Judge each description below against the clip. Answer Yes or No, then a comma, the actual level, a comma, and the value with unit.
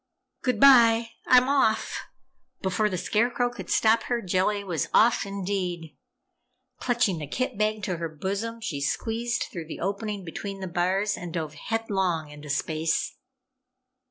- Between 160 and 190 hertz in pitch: No, high, 200 Hz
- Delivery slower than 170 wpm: Yes, average, 140 wpm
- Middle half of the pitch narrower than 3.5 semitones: No, average, 4.8 semitones